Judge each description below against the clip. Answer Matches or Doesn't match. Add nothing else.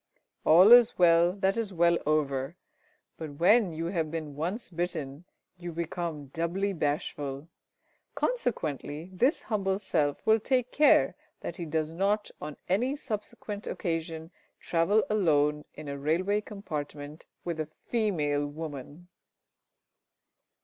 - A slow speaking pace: Matches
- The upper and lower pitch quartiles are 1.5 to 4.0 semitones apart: Doesn't match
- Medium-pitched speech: Matches